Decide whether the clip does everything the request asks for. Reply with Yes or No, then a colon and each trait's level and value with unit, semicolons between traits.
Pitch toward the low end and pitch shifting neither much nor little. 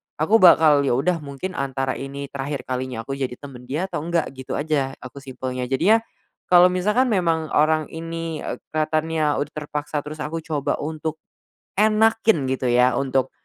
No: medium, 150 Hz; average, 3.5 semitones